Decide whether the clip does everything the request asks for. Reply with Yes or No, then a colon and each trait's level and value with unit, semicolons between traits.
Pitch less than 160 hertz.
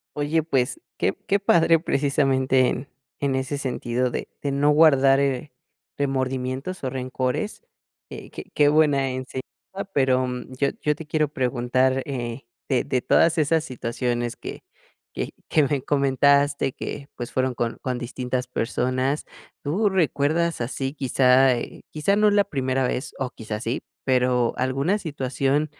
Yes: low, 135 Hz